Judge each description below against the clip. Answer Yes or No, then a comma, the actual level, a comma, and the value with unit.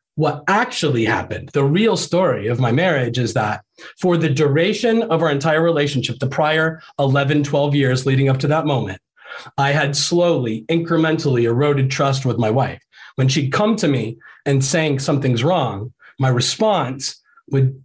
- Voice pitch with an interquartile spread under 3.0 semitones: No, average, 3.6 semitones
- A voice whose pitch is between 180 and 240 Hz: No, medium, 140 Hz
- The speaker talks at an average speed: Yes, average, 165 wpm